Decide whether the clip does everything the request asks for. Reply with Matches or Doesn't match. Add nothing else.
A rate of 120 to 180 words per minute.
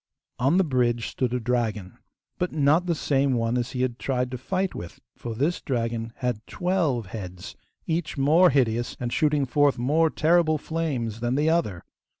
Matches